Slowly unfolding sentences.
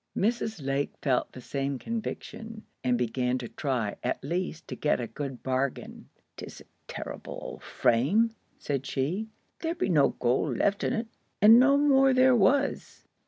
No: average, 160 wpm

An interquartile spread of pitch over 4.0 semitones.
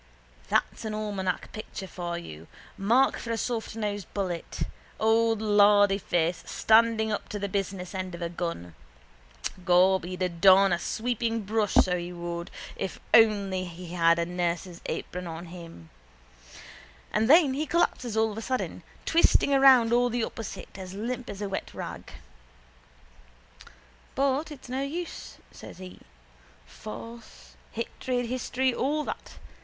Yes: average, 4.5 semitones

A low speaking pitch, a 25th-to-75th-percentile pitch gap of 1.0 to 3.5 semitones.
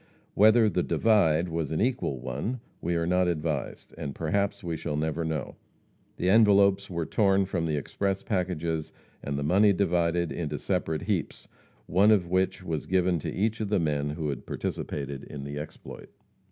No: very low, 85 Hz; average, 4.2 semitones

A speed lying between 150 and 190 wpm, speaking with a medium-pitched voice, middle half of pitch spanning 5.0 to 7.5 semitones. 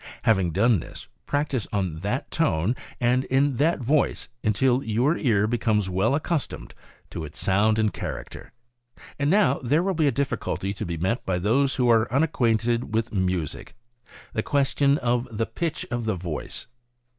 No: average, 170 wpm; low, 120 Hz; average, 5.3 semitones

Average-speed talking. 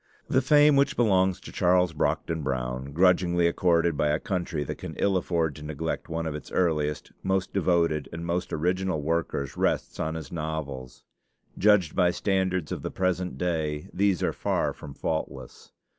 Yes: average, 170 wpm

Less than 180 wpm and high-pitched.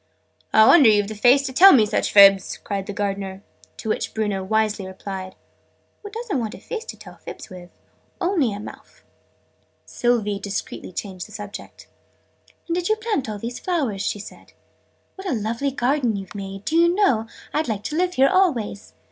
No: average, 185 wpm; high, 220 Hz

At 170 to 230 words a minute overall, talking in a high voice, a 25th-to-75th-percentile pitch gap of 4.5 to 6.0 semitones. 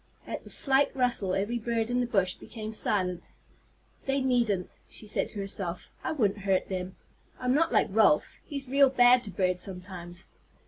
Yes: average, 175 wpm; high, 215 Hz; average, 4.9 semitones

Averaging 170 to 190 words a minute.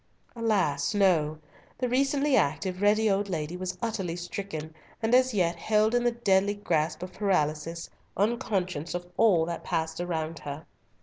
No: average, 150 wpm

